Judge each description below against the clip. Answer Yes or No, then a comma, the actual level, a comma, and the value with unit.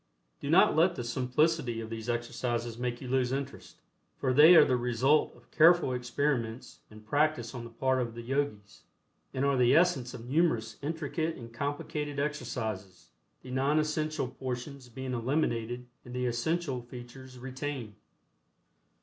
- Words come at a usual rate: Yes, average, 155 wpm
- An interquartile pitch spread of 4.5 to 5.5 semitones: No, average, 3.4 semitones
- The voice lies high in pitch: No, low, 130 Hz